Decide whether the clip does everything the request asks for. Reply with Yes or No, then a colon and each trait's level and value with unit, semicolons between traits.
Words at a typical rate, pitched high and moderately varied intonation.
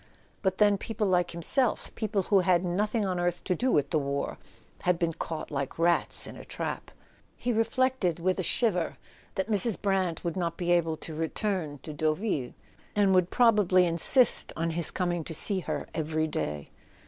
No: average, 180 wpm; medium, 180 Hz; average, 3.8 semitones